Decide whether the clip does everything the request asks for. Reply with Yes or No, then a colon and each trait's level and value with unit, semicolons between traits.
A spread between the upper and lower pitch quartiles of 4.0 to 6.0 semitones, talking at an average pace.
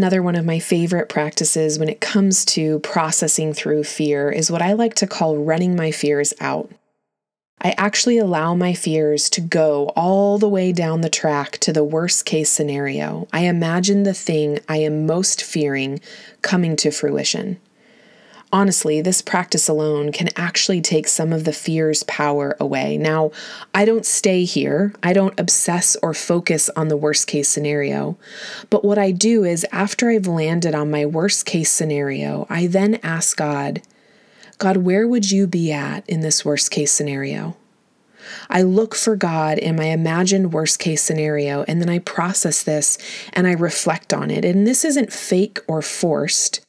Yes: average, 4.4 semitones; average, 170 wpm